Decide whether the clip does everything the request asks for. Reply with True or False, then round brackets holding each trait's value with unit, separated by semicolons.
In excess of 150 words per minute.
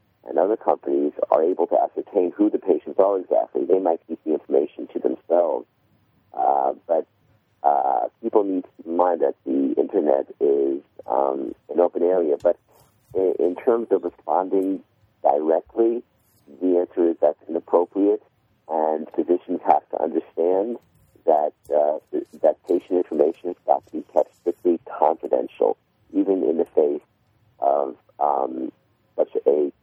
False (145 wpm)